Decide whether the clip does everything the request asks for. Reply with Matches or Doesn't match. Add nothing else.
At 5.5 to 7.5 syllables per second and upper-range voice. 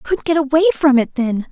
Matches